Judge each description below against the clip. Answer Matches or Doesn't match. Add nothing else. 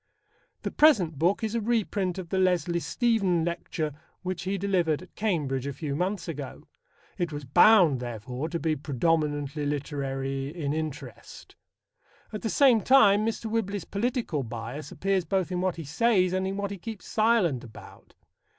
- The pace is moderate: Matches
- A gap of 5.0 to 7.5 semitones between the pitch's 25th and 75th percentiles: Matches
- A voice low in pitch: Doesn't match